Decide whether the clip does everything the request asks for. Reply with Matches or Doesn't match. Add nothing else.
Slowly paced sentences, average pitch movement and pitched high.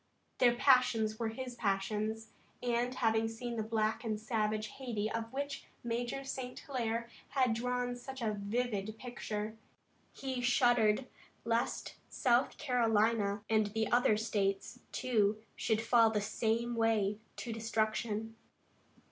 Doesn't match